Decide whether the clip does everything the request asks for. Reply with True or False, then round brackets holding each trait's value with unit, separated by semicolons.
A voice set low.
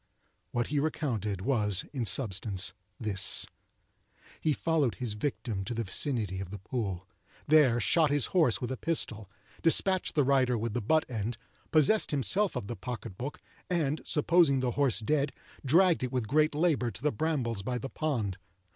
True (130 Hz)